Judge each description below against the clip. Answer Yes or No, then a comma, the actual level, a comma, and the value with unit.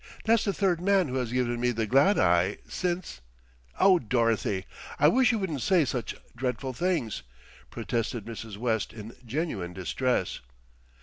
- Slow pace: No, average, 160 wpm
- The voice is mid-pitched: No, low, 125 Hz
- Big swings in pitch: Yes, wide, 7.8 semitones